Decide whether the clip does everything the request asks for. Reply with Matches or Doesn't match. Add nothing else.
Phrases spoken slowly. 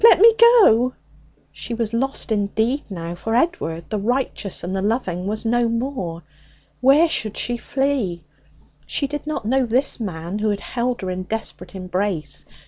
Doesn't match